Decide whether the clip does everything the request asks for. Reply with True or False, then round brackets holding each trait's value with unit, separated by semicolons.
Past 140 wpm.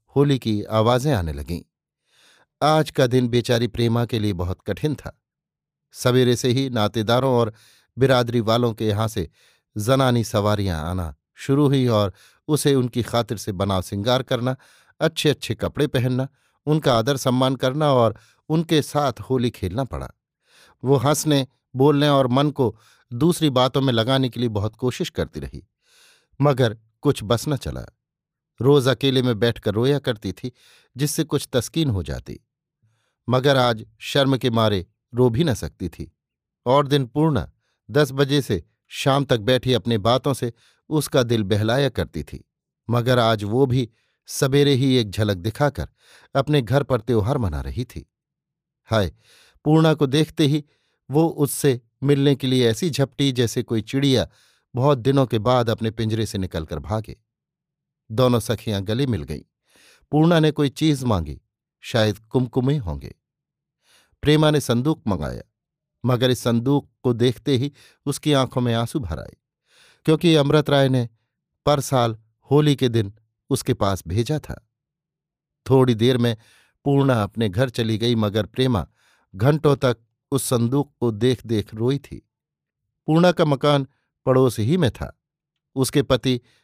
True (155 wpm)